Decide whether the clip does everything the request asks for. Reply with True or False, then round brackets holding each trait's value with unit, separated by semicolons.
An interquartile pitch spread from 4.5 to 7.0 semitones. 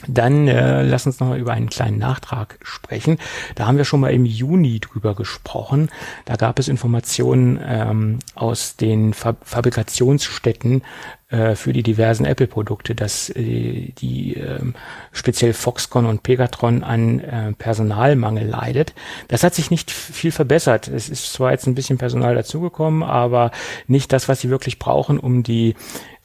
False (3.0 semitones)